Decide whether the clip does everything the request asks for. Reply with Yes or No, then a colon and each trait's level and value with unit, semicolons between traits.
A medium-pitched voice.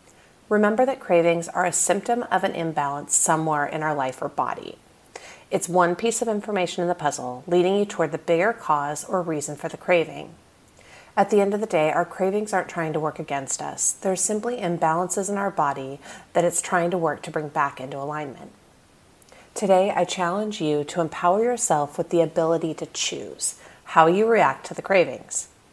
Yes: medium, 175 Hz